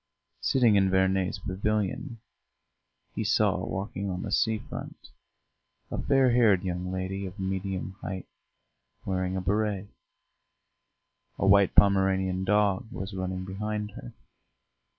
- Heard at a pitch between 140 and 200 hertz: No, very low, 95 Hz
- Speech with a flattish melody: Yes, narrow, 1.9 semitones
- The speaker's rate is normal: No, slow, 120 wpm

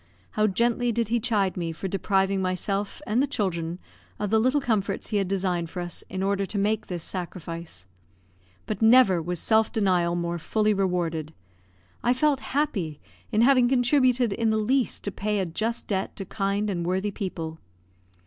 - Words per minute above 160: Yes, average, 175 wpm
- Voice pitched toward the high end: Yes, high, 200 Hz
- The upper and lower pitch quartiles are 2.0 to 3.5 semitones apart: No, average, 3.9 semitones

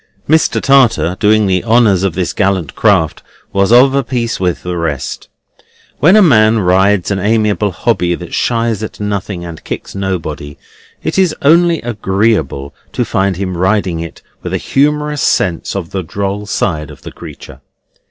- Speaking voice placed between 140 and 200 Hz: No, low, 100 Hz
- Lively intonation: No, average, 4.4 semitones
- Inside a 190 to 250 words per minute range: No, average, 165 wpm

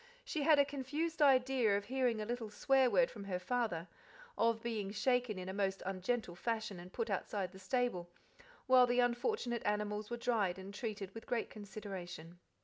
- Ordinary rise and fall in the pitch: Yes, average, 4.2 semitones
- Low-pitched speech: No, high, 220 Hz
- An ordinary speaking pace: Yes, average, 180 wpm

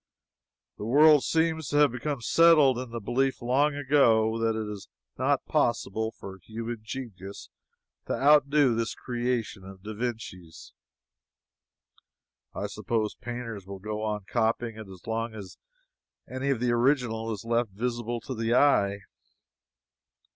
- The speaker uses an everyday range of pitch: Yes, average, 3.2 semitones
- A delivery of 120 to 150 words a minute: Yes, average, 140 wpm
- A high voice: No, low, 115 Hz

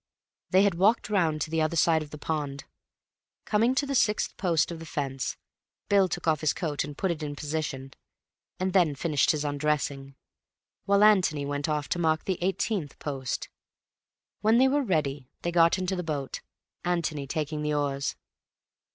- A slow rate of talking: No, average, 175 wpm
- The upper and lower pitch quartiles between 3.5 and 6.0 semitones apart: Yes, average, 4.2 semitones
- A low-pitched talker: No, medium, 155 Hz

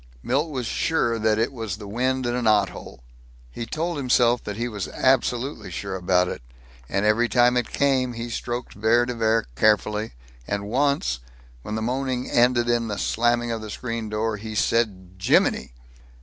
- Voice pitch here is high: No, low, 115 Hz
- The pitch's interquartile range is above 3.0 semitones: No, narrow, 2.6 semitones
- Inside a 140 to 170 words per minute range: No, average, 180 wpm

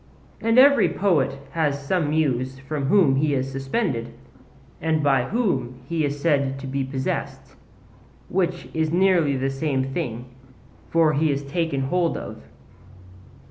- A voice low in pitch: No, medium, 145 Hz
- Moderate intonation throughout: Yes, average, 3.7 semitones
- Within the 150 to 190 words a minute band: No, average, 140 wpm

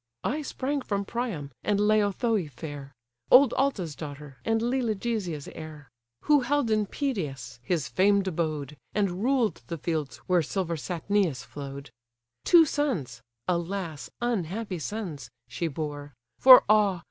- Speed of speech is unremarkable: No, slow, 130 wpm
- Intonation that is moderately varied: No, wide, 7.0 semitones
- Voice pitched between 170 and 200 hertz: Yes, medium, 185 Hz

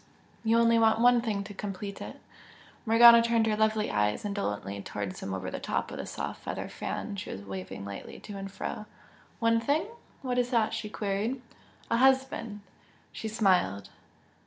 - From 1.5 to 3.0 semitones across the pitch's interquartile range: No, average, 3.9 semitones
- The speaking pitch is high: Yes, high, 215 Hz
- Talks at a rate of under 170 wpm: No, average, 175 wpm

